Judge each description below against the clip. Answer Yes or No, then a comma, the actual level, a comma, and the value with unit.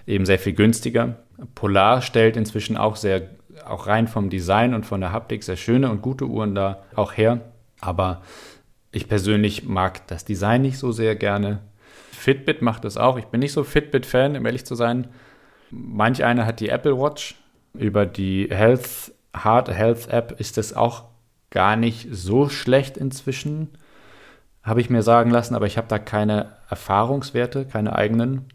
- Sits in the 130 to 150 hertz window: No, low, 115 Hz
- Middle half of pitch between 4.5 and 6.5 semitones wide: No, average, 3.3 semitones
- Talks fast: No, average, 170 wpm